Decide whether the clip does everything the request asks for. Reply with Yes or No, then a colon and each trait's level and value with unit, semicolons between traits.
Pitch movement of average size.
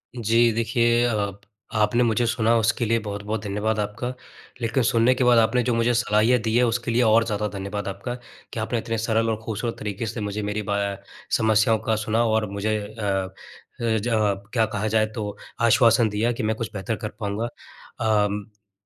No: narrow, 1.9 semitones